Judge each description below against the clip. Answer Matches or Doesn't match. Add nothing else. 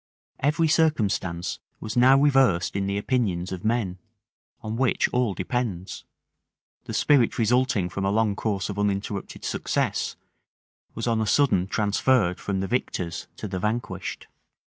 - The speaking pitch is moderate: Doesn't match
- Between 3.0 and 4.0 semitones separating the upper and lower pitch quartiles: Doesn't match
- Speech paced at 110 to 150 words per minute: Matches